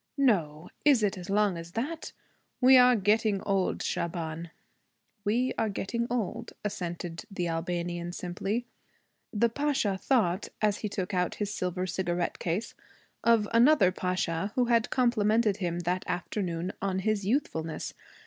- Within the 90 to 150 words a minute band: Yes, average, 140 wpm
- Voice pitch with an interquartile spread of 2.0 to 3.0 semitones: No, average, 4.6 semitones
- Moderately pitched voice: No, high, 195 Hz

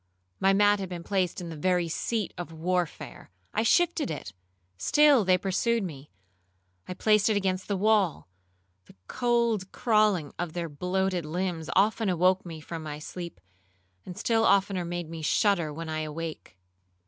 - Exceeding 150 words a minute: No, average, 145 wpm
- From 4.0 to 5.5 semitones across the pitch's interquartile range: Yes, average, 4.4 semitones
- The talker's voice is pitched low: No, medium, 180 Hz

